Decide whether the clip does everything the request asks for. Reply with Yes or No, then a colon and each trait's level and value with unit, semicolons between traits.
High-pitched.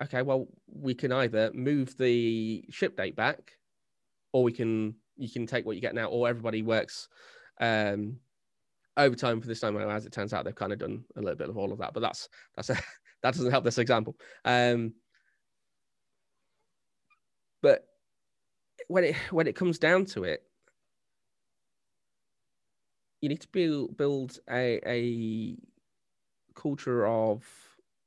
No: low, 120 Hz